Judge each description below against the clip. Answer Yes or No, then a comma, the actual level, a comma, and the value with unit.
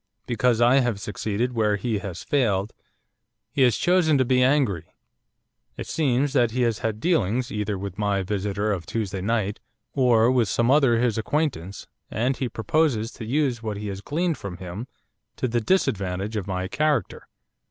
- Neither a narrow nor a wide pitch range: Yes, average, 4.1 semitones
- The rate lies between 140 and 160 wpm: No, average, 175 wpm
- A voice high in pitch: No, low, 115 Hz